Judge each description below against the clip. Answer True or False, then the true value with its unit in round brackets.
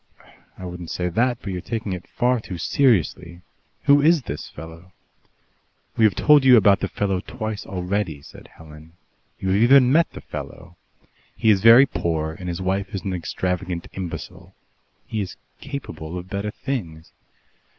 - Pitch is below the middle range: True (95 Hz)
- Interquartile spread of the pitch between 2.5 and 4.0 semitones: False (4.8 semitones)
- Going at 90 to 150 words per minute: False (165 wpm)